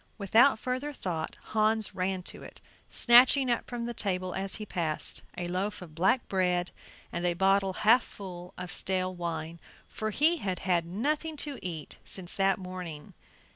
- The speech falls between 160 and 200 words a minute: Yes, average, 170 wpm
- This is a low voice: No, high, 190 Hz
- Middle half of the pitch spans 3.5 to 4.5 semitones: Yes, average, 4.1 semitones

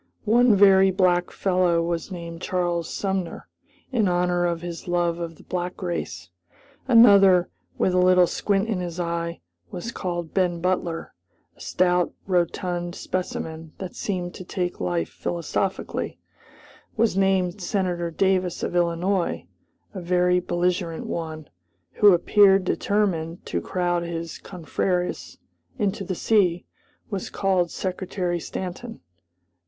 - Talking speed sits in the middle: No, slow, 125 wpm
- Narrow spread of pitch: Yes, narrow, 1.8 semitones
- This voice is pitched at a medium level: Yes, medium, 180 Hz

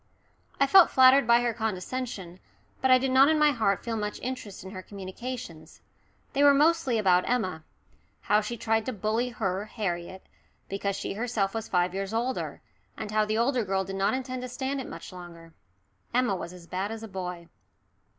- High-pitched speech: Yes, high, 215 Hz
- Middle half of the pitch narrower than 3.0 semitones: No, average, 5.0 semitones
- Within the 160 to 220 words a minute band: Yes, average, 190 wpm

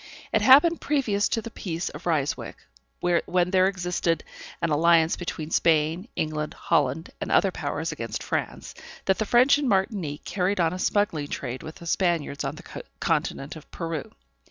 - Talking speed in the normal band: Yes, average, 165 wpm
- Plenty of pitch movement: No, average, 4.1 semitones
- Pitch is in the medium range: Yes, medium, 175 Hz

